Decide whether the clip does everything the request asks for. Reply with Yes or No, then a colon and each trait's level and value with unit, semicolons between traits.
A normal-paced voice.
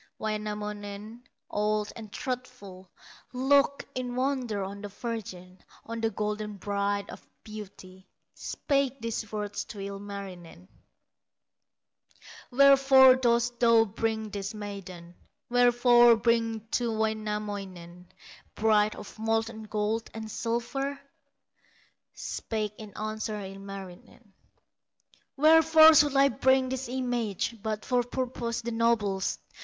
No: slow, 105 wpm